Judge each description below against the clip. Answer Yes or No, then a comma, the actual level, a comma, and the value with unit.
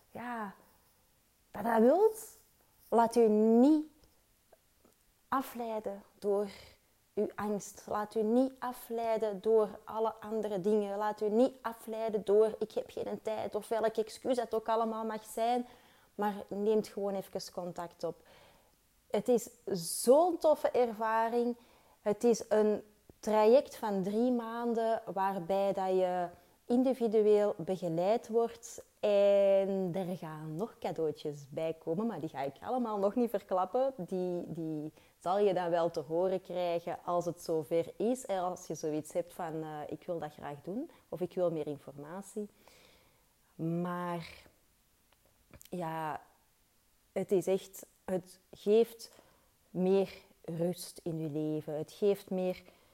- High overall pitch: Yes, high, 205 Hz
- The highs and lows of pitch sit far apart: No, average, 4.3 semitones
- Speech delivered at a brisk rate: No, slow, 135 wpm